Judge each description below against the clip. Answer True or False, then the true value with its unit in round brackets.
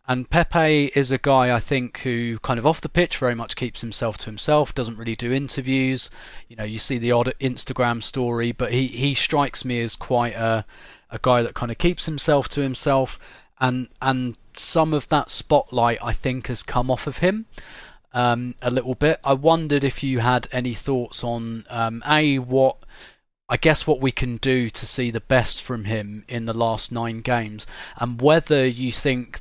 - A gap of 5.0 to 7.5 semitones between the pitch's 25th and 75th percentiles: False (2.7 semitones)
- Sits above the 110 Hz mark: True (125 Hz)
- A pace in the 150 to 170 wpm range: False (200 wpm)